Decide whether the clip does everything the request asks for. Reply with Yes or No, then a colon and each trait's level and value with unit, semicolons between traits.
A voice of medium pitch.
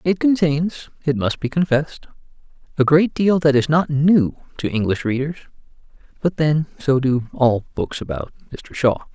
Yes: medium, 145 Hz